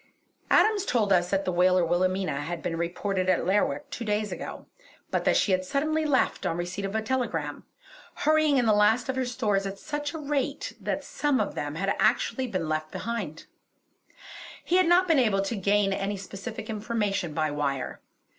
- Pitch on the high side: Yes, high, 205 Hz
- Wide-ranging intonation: Yes, wide, 6.0 semitones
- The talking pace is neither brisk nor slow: Yes, average, 190 wpm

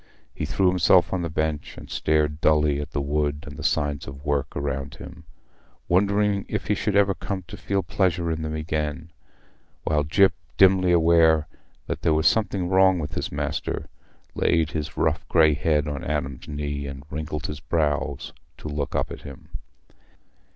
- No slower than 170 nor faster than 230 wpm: Yes, average, 175 wpm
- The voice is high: No, very low, 80 Hz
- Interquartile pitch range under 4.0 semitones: Yes, average, 3.3 semitones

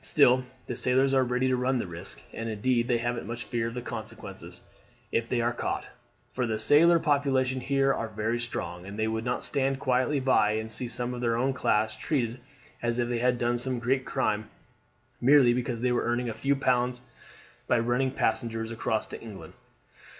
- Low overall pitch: Yes, low, 120 Hz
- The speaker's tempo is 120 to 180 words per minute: No, average, 200 wpm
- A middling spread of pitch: No, narrow, 2.3 semitones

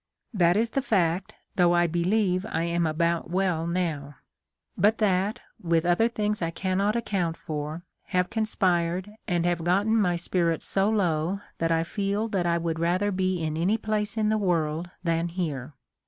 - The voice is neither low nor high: Yes, medium, 175 Hz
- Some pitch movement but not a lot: Yes, average, 3.3 semitones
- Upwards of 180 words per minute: No, average, 170 wpm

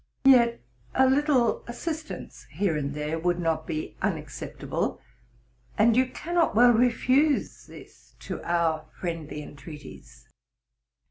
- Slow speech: Yes, slow, 115 wpm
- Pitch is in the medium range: No, high, 205 Hz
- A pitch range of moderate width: No, wide, 8.6 semitones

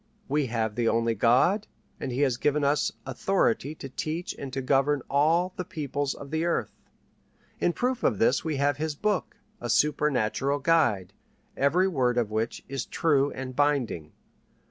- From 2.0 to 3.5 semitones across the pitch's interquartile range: No, average, 4.1 semitones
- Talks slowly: No, average, 165 wpm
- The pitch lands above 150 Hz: No, medium, 140 Hz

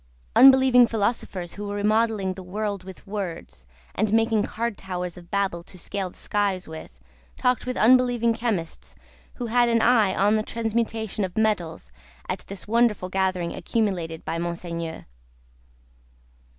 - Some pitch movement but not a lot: Yes, average, 3.9 semitones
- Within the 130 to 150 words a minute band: Yes, average, 145 wpm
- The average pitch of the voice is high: Yes, high, 205 Hz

